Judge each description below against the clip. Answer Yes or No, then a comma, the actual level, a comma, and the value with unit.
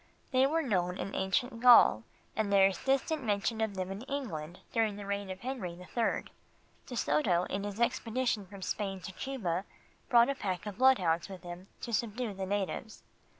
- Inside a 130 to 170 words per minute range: No, average, 190 wpm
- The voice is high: Yes, high, 205 Hz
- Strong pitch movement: No, average, 4.2 semitones